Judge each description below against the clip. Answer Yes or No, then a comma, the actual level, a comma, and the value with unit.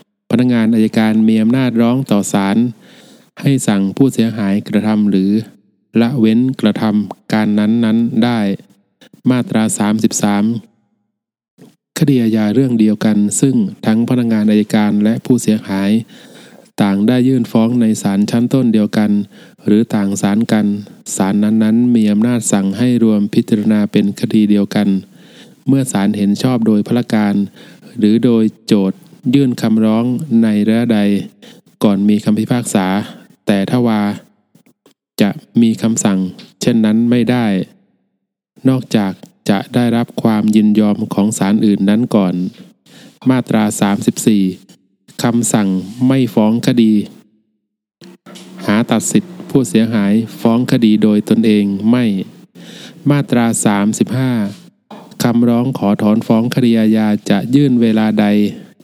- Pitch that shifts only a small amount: Yes, narrow, 2.3 semitones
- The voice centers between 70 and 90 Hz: No, low, 110 Hz